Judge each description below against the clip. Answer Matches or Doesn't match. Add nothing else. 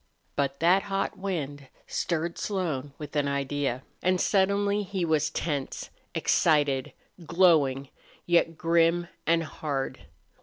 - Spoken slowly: Matches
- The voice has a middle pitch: Matches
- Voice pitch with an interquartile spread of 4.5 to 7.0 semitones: Doesn't match